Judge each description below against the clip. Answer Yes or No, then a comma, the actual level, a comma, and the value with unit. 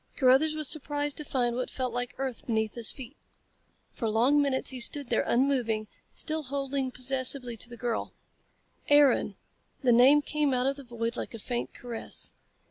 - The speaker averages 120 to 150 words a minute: No, average, 175 wpm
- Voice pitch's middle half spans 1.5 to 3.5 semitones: Yes, average, 2.8 semitones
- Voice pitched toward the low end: No, very high, 255 Hz